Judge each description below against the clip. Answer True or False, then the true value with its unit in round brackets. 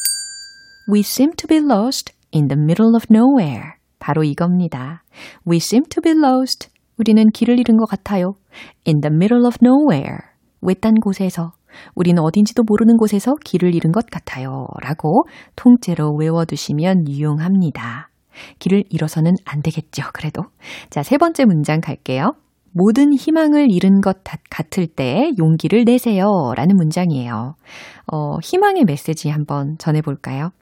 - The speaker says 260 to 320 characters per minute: False (365 characters per minute)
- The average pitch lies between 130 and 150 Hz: False (185 Hz)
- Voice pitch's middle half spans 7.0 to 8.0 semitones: True (7.4 semitones)